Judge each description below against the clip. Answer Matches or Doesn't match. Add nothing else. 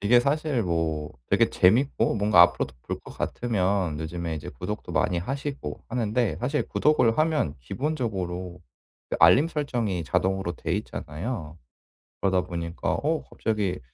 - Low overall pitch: Matches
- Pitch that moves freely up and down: Matches